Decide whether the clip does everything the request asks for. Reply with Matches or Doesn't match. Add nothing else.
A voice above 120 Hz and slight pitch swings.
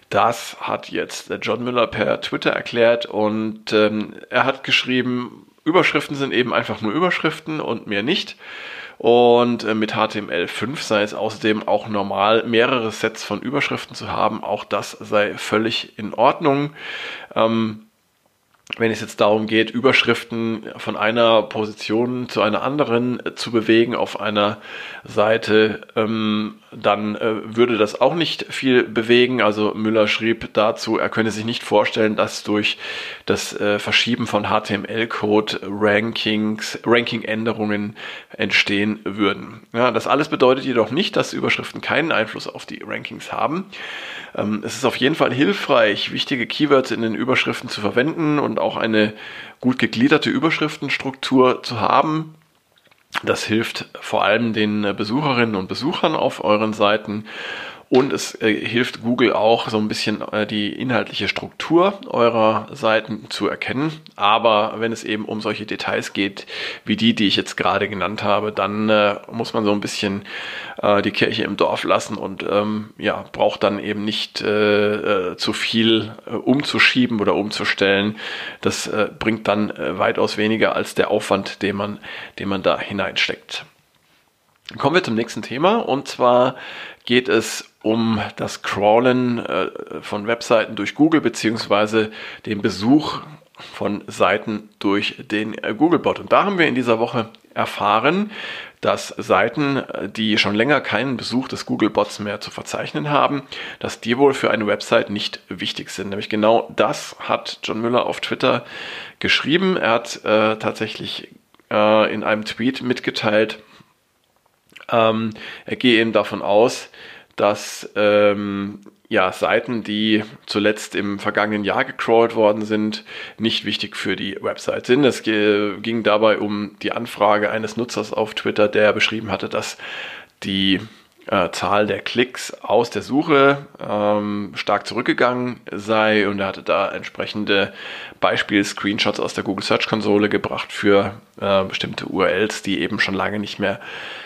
Doesn't match